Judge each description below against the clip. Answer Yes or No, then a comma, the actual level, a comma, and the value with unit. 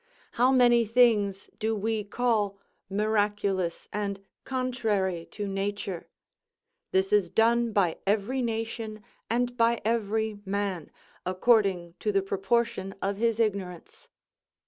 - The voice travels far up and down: No, average, 2.8 semitones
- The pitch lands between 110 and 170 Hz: No, high, 210 Hz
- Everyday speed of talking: No, slow, 115 wpm